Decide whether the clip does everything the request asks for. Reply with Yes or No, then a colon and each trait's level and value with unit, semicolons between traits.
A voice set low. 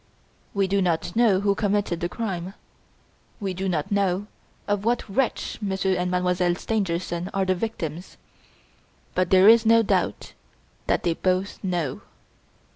No: high, 190 Hz